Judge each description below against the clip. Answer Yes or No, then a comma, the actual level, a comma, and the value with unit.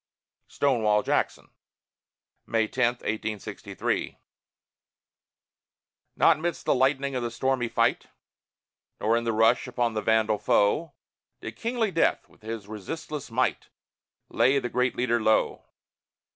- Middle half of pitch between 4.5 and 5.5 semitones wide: No, average, 3.3 semitones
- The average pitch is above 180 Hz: No, low, 120 Hz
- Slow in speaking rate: Yes, slow, 120 wpm